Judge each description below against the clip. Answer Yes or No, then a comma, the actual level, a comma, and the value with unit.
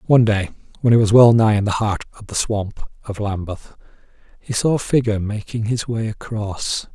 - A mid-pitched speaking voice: No, low, 110 Hz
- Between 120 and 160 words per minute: No, average, 200 wpm